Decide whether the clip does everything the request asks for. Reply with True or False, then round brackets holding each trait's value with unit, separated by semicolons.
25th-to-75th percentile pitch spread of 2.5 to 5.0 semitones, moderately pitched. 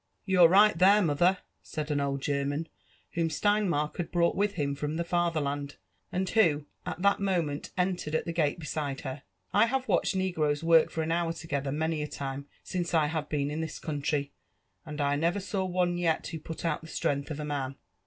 True (3.5 semitones; 160 Hz)